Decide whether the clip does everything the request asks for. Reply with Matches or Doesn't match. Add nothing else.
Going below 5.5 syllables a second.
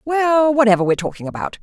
Doesn't match